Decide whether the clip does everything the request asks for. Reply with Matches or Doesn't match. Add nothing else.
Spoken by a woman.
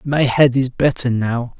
Doesn't match